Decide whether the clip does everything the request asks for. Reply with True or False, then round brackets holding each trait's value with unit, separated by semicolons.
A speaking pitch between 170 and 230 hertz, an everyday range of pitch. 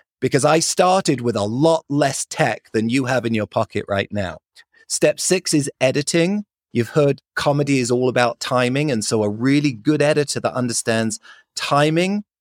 False (140 Hz; 4.5 semitones)